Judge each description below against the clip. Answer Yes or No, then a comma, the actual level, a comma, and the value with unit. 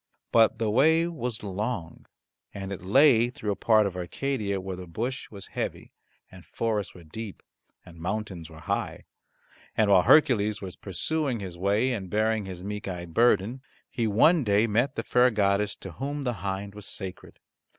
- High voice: No, low, 105 Hz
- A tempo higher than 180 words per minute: No, average, 175 wpm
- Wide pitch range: No, average, 3.8 semitones